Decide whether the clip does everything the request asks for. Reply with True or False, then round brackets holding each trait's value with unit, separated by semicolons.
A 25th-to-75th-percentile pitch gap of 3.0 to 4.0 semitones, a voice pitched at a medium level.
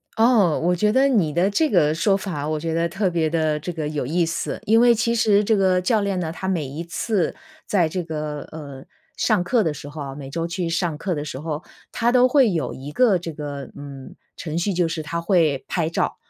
False (4.6 semitones; 170 Hz)